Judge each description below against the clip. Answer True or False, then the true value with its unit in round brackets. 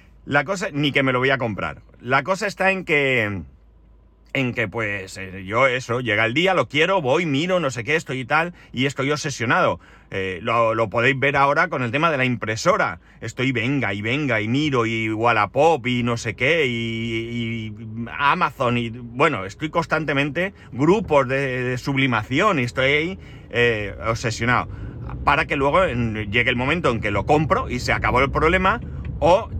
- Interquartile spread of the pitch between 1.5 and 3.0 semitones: False (4.1 semitones)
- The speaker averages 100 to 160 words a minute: False (185 wpm)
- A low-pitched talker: True (125 Hz)